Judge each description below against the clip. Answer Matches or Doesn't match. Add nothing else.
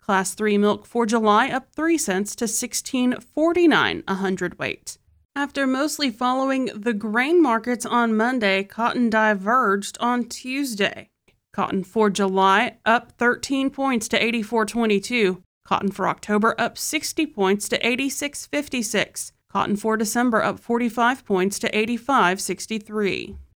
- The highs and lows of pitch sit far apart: Doesn't match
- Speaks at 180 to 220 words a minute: Doesn't match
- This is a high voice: Matches